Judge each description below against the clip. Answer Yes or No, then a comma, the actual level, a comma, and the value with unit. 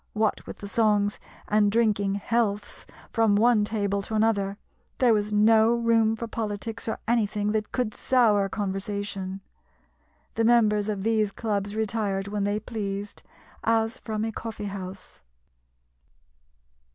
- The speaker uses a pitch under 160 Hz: No, high, 210 Hz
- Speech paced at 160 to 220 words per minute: No, slow, 135 wpm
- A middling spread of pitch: No, narrow, 1.8 semitones